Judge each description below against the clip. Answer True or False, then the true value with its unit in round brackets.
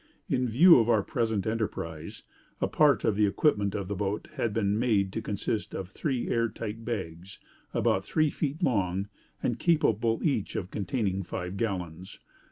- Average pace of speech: True (170 wpm)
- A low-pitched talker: True (105 Hz)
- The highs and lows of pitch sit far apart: False (3.4 semitones)